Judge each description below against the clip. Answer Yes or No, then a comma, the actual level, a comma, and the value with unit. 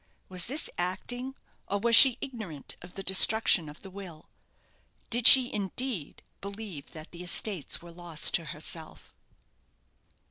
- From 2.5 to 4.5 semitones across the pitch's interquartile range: No, average, 5.1 semitones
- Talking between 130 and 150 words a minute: Yes, average, 140 wpm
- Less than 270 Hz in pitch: Yes, high, 190 Hz